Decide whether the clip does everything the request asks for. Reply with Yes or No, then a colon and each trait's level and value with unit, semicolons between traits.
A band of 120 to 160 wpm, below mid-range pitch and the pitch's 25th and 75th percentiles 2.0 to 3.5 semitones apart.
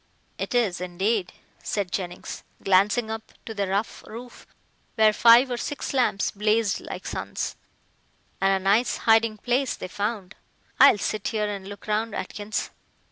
No: average, 150 wpm; high, 210 Hz; narrow, 2.6 semitones